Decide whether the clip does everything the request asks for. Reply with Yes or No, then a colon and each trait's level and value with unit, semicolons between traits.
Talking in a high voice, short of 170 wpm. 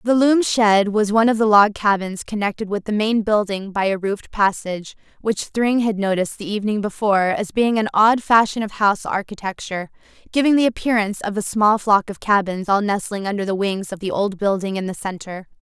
No: high, 205 Hz; fast, 205 wpm